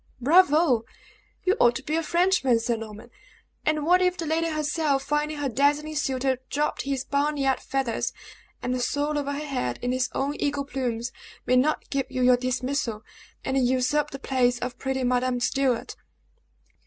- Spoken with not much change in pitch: No, average, 3.0 semitones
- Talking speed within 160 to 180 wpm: Yes, average, 165 wpm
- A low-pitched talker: No, very high, 270 Hz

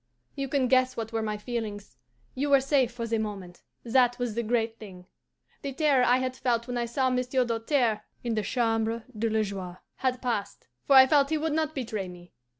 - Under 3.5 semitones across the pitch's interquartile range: Yes, average, 2.9 semitones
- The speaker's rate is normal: No, fast, 210 wpm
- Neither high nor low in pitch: No, high, 235 Hz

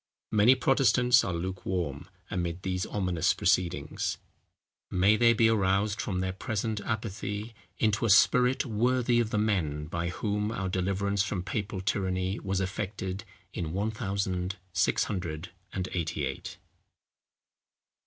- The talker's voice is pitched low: Yes, low, 100 Hz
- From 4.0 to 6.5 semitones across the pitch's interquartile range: No, average, 2.9 semitones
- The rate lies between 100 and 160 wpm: Yes, slow, 135 wpm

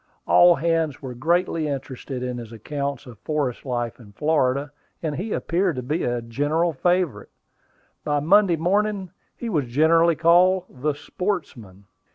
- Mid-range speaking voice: Yes, medium, 150 Hz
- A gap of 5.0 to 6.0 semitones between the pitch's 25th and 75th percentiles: Yes, average, 5.3 semitones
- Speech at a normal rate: Yes, average, 150 wpm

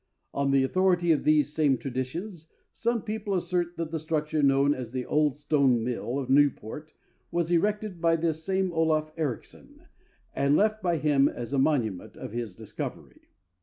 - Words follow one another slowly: No, average, 165 wpm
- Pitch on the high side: No, medium, 155 Hz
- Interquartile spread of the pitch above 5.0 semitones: No, average, 4.0 semitones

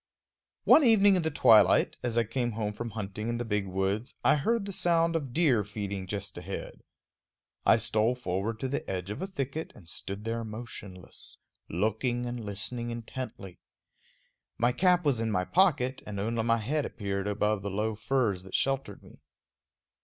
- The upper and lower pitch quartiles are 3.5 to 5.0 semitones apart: Yes, average, 4.4 semitones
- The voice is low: Yes, low, 115 Hz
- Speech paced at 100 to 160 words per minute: No, average, 175 wpm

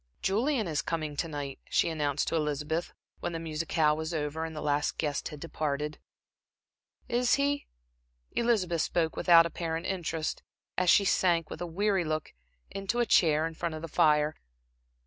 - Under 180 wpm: Yes, average, 165 wpm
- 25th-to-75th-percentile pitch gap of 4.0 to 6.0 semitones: No, average, 2.8 semitones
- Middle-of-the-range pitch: Yes, medium, 165 Hz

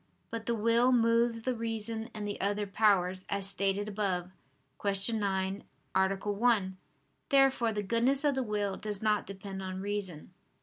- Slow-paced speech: No, average, 160 wpm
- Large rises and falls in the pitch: No, average, 2.9 semitones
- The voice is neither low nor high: No, high, 205 Hz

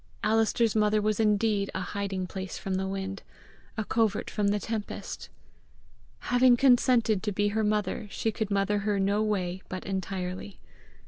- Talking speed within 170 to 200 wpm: No, average, 155 wpm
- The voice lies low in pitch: No, high, 205 Hz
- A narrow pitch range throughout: Yes, narrow, 2.0 semitones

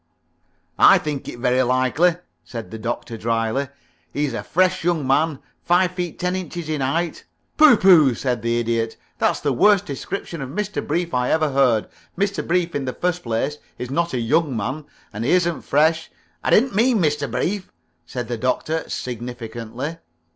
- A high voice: No, medium, 145 Hz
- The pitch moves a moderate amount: No, wide, 6.0 semitones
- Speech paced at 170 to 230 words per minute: Yes, average, 180 wpm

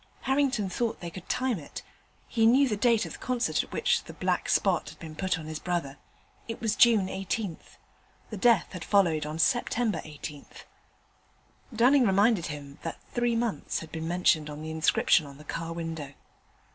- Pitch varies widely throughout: Yes, wide, 6.7 semitones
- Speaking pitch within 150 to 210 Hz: Yes, medium, 185 Hz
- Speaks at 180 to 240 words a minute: Yes, average, 185 wpm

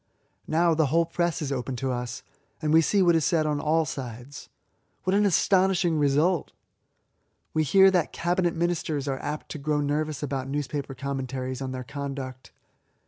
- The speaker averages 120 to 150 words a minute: No, average, 170 wpm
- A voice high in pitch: No, medium, 150 Hz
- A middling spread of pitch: Yes, average, 3.8 semitones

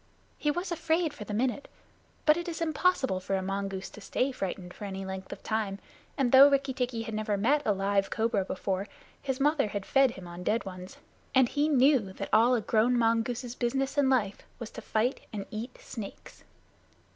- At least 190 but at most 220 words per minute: Yes, average, 200 wpm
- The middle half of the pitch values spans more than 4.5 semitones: Yes, wide, 5.4 semitones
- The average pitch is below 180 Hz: No, high, 230 Hz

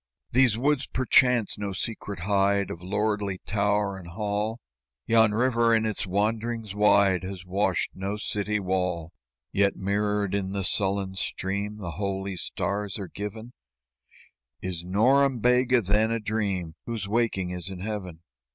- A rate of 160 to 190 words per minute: No, average, 140 wpm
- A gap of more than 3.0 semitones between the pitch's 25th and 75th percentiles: No, narrow, 2.5 semitones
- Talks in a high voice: No, low, 100 Hz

